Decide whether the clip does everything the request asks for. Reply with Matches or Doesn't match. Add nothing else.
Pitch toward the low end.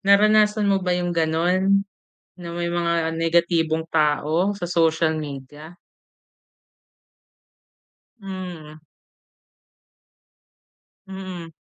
Doesn't match